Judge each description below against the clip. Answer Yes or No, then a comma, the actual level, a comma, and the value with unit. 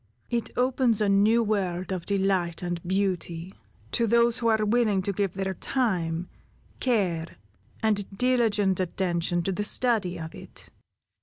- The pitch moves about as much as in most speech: Yes, average, 4.1 semitones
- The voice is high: Yes, high, 195 Hz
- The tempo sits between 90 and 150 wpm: Yes, average, 145 wpm